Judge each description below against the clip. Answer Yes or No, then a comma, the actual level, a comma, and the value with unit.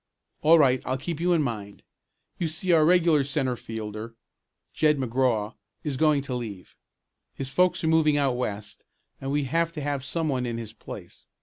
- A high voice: No, low, 135 Hz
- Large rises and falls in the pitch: No, average, 4.6 semitones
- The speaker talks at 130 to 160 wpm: No, average, 185 wpm